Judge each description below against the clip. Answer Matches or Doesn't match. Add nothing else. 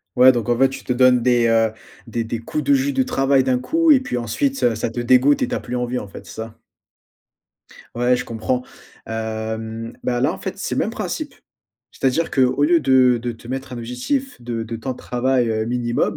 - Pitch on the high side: Doesn't match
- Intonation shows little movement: Matches